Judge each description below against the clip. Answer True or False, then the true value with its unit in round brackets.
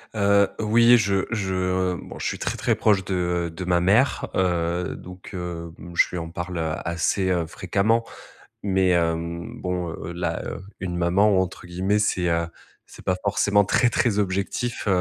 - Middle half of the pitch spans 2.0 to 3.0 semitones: True (2.7 semitones)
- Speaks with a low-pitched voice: True (95 Hz)